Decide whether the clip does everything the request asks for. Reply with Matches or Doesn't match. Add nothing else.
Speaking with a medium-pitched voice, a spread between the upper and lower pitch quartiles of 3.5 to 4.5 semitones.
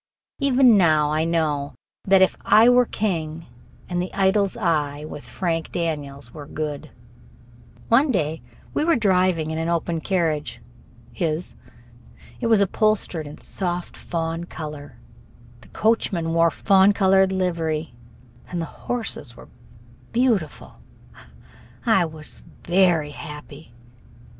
Matches